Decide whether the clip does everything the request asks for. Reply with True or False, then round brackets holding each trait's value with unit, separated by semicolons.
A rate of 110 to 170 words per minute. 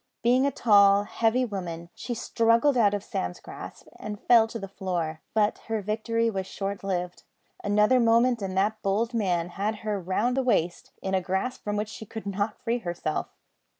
False (185 wpm)